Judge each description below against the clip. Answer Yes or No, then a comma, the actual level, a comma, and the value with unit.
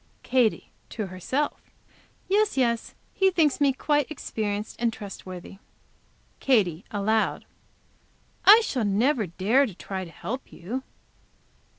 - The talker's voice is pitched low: No, high, 225 Hz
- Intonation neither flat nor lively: No, wide, 5.9 semitones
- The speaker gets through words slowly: Yes, slow, 115 wpm